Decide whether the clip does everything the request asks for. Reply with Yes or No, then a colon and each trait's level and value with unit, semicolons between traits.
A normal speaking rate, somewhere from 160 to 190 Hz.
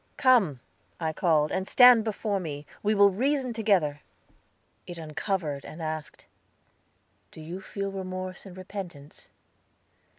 No: slow, 125 wpm; medium, 185 Hz